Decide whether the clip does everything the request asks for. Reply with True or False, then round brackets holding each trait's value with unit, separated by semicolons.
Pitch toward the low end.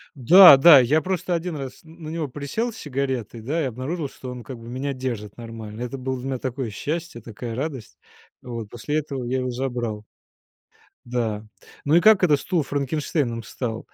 True (130 Hz)